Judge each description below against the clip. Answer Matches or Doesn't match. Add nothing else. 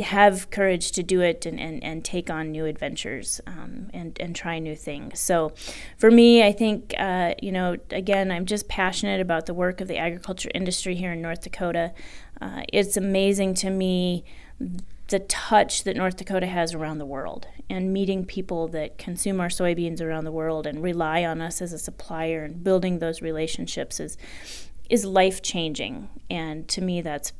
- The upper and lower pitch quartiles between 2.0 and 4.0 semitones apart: Matches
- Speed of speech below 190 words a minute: Matches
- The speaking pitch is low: Doesn't match